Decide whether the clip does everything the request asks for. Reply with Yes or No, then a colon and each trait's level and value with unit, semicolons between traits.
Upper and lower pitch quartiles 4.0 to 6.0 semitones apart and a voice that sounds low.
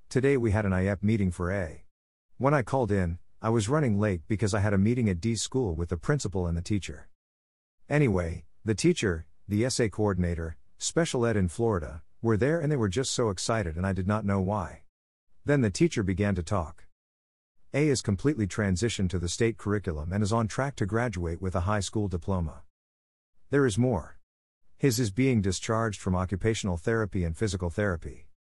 Yes: average, 4.7 semitones; low, 100 Hz